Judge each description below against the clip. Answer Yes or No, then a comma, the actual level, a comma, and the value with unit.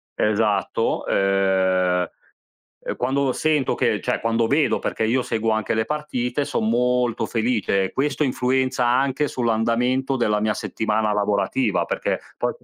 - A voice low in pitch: Yes, low, 115 Hz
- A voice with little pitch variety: No, average, 3.6 semitones